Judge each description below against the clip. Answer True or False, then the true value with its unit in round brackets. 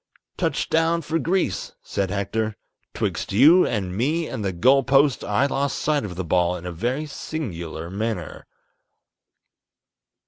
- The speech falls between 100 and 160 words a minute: True (145 wpm)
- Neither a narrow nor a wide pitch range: False (7.8 semitones)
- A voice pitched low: True (115 Hz)